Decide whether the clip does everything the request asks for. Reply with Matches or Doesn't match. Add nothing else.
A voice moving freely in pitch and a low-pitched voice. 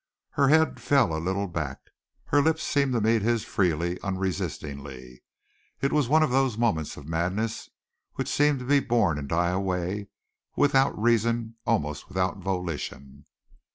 Matches